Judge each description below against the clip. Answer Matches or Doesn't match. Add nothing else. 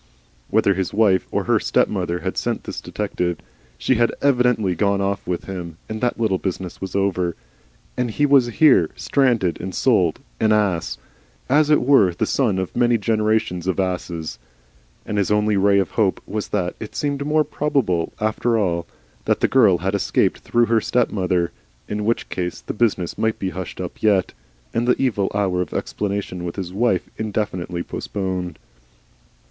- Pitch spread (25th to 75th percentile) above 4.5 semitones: Doesn't match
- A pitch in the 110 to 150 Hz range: Doesn't match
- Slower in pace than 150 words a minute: Doesn't match